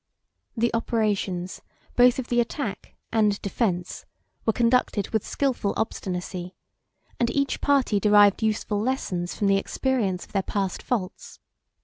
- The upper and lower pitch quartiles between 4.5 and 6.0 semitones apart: No, average, 3.7 semitones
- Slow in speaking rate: Yes, slow, 130 wpm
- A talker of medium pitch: No, high, 210 Hz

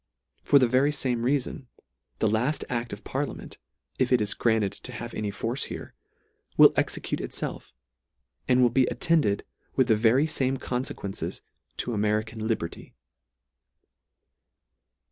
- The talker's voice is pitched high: No, low, 120 Hz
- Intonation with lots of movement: No, average, 3.2 semitones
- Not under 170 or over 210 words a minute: No, slow, 135 wpm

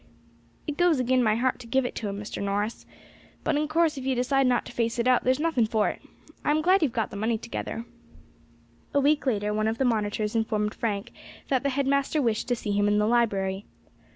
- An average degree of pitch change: Yes, average, 4.2 semitones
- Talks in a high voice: Yes, high, 235 Hz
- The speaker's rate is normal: No, fast, 235 wpm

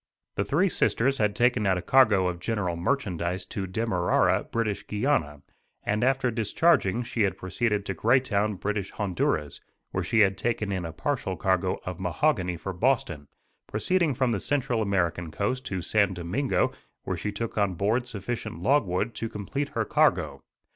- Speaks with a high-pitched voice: No, low, 105 Hz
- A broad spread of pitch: No, average, 4.7 semitones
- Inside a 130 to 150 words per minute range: No, average, 165 wpm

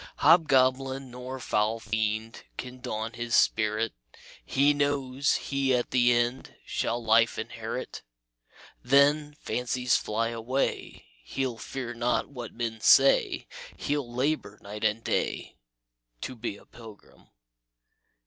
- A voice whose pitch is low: Yes, low, 120 Hz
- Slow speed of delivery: Yes, slow, 120 wpm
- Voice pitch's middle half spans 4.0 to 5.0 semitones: No, average, 2.9 semitones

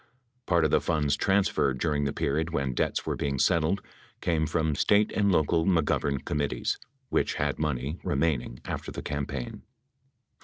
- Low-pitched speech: Yes, very low, 75 Hz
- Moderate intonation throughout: Yes, average, 3.0 semitones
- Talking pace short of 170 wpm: Yes, average, 160 wpm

